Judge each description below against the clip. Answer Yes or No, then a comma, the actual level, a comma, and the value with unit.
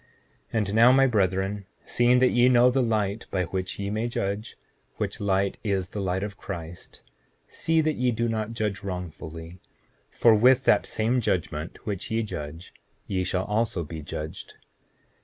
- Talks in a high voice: No, low, 100 Hz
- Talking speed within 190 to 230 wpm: No, average, 170 wpm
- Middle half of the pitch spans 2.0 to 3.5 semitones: No, average, 4.1 semitones